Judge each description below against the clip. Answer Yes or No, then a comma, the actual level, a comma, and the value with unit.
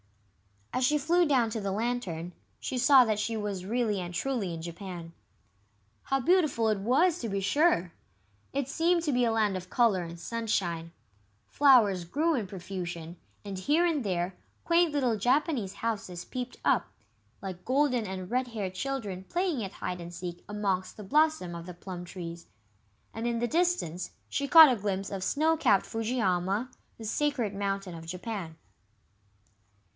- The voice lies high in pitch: Yes, high, 215 Hz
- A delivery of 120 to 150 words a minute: No, average, 165 wpm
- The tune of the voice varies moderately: No, wide, 6.4 semitones